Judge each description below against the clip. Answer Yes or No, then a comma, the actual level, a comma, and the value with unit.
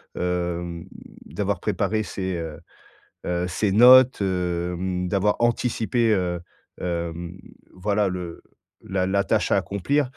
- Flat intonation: No, average, 3.0 semitones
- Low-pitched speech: Yes, very low, 95 Hz